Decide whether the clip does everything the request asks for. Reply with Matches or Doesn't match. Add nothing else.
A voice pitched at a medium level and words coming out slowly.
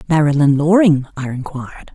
Matches